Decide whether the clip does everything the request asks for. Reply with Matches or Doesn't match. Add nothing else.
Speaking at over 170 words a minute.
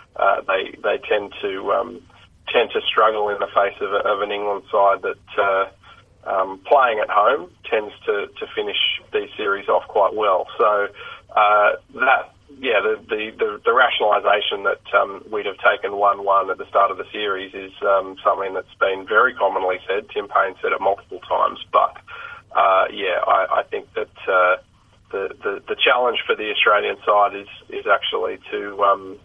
Matches